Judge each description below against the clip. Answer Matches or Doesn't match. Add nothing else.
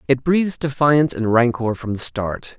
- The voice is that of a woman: Doesn't match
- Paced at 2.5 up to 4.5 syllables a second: Doesn't match